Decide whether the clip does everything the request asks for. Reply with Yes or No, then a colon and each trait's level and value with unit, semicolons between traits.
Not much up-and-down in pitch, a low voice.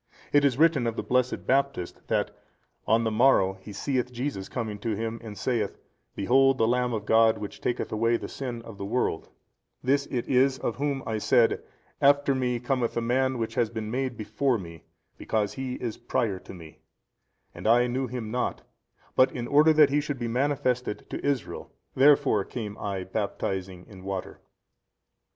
No: average, 3.5 semitones; low, 120 Hz